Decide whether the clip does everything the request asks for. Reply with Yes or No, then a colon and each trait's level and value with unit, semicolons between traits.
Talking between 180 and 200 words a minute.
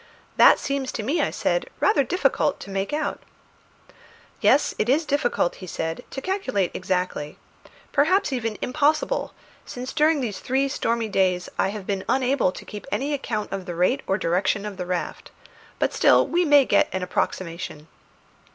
No: average, 170 wpm